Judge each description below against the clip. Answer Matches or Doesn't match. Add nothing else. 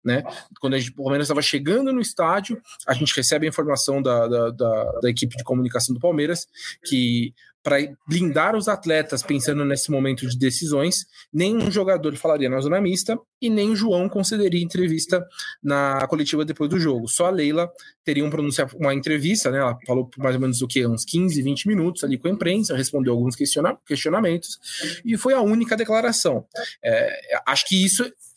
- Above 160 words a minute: Matches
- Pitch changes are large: Matches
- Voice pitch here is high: Doesn't match